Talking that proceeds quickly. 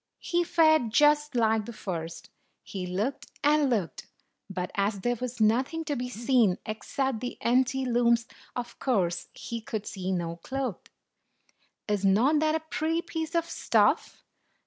No: average, 150 wpm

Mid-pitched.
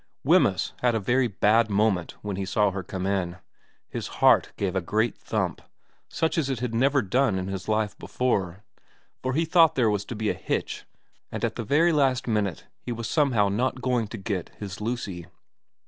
No: low, 110 Hz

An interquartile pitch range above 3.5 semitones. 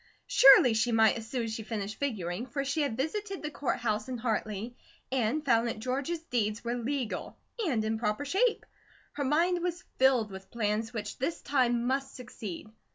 Yes: average, 4.1 semitones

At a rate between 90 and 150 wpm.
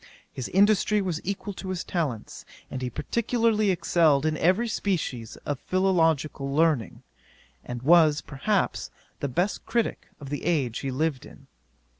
Yes: average, 145 wpm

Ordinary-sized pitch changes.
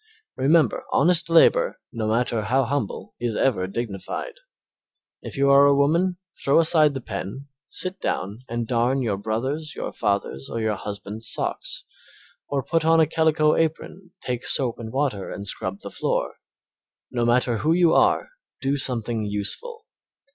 No: wide, 6.0 semitones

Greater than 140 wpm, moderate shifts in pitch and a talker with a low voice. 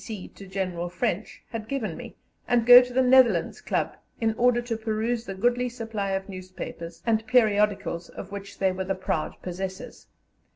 No: average, 175 wpm; average, 4.0 semitones; high, 215 Hz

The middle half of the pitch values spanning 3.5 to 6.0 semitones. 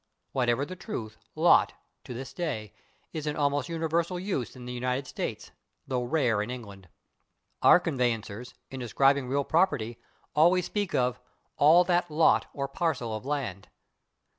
Yes: average, 5.1 semitones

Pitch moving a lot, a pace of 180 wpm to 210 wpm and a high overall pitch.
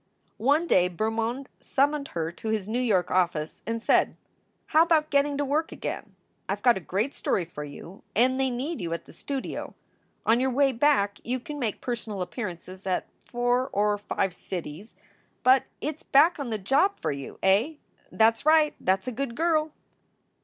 Yes: wide, 6.6 semitones; average, 190 wpm; high, 240 Hz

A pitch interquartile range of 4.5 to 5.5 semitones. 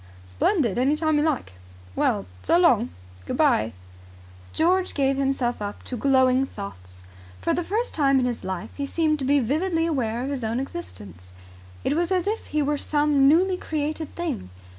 Yes: average, 5.1 semitones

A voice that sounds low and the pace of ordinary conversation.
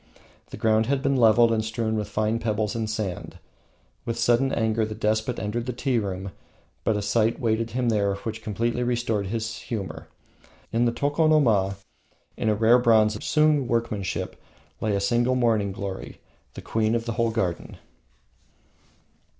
Yes: low, 110 Hz; average, 165 wpm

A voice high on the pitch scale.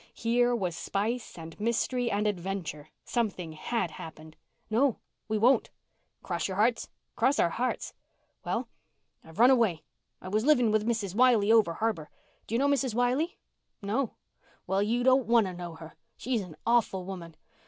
Yes: high, 215 Hz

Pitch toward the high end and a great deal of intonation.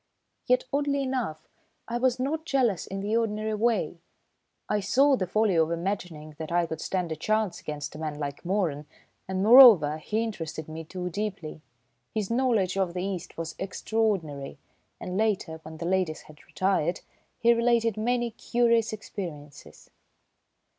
Yes: high, 195 Hz; wide, 6.0 semitones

